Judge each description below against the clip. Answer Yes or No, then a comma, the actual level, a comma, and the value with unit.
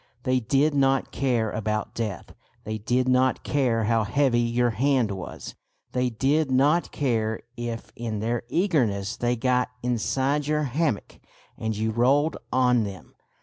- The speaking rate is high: No, average, 145 wpm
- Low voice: Yes, low, 125 Hz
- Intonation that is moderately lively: Yes, average, 3.4 semitones